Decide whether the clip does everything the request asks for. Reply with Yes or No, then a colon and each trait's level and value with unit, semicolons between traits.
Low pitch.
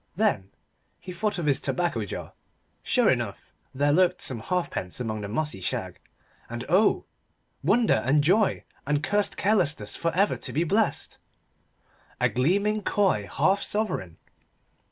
No: medium, 170 Hz